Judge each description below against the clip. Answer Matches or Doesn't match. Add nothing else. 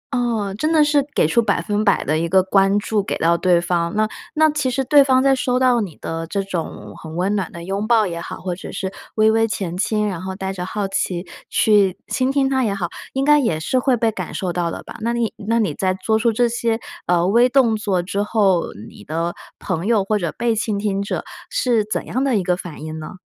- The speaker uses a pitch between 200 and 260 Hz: Matches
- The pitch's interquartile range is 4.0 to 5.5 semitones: Matches